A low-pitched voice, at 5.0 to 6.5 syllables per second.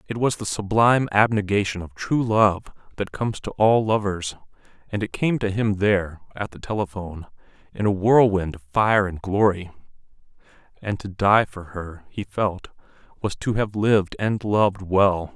No: low, 100 Hz; 4.8 syllables/s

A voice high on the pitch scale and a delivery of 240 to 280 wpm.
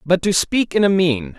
No: medium, 170 Hz; fast, 260 wpm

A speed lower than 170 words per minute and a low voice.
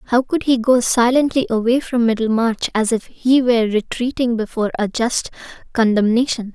No: average, 155 wpm; high, 235 Hz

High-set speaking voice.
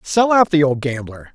No: medium, 155 Hz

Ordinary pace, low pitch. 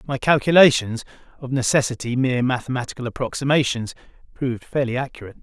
No: slow, 90 wpm; low, 130 Hz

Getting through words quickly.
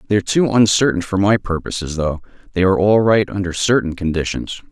No: average, 180 wpm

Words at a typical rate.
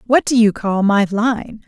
No: fast, 215 wpm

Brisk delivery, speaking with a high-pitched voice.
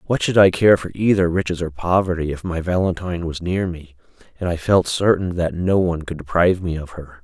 No: fast, 225 wpm; very low, 90 Hz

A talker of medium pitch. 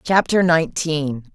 Yes: medium, 160 Hz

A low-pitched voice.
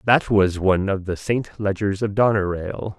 Yes: low, 100 Hz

